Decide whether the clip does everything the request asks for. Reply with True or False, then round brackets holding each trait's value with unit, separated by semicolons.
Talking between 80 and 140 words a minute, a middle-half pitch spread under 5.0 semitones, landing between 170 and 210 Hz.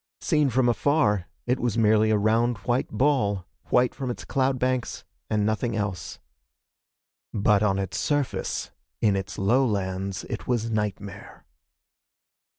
False (135 wpm; 3.7 semitones; 110 Hz)